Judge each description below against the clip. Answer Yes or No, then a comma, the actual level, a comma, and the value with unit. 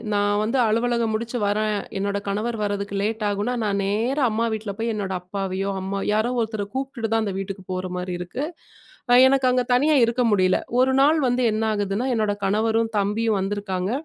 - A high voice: Yes, high, 215 Hz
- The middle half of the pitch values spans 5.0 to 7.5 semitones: No, average, 2.8 semitones